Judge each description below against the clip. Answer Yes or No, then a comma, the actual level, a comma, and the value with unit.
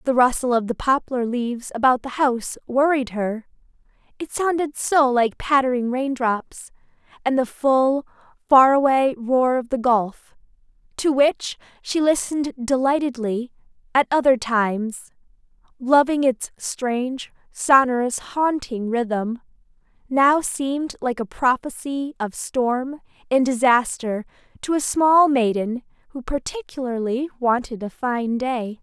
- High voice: Yes, very high, 255 Hz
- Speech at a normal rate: No, slow, 120 wpm